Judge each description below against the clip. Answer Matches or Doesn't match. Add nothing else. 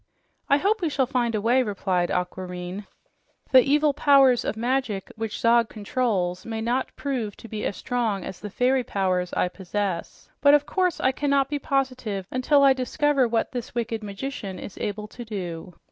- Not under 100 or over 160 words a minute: Doesn't match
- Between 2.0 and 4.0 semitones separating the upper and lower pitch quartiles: Doesn't match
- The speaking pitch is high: Matches